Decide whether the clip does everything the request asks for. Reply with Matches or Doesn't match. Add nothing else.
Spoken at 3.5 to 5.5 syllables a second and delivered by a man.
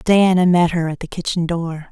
Doesn't match